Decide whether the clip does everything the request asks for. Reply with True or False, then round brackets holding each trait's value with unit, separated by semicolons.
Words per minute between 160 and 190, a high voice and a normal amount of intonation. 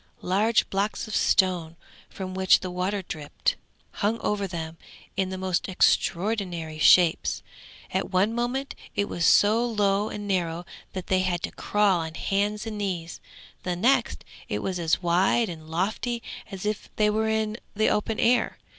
True (165 wpm; 195 Hz; 3.2 semitones)